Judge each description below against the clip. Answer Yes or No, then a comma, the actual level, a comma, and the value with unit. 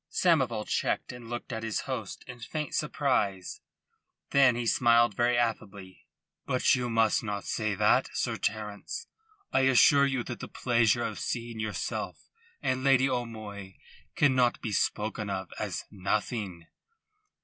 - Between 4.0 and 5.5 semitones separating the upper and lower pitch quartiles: No, average, 3.3 semitones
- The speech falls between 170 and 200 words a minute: No, average, 140 wpm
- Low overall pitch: Yes, low, 115 Hz